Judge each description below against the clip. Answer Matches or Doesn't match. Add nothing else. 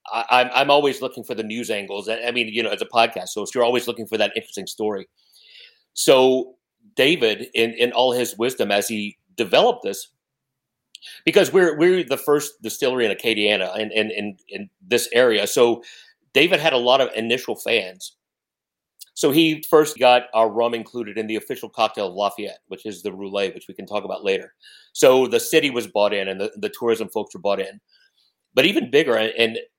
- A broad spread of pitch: Matches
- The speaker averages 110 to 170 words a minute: Doesn't match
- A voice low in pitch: Matches